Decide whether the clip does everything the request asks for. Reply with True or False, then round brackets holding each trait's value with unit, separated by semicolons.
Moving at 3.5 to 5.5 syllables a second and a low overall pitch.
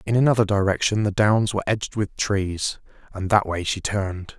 True (5.4 syllables/s; 100 Hz)